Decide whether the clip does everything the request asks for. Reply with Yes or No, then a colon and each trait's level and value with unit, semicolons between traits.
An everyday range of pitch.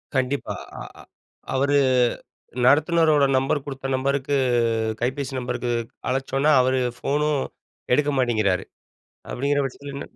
No: narrow, 1.8 semitones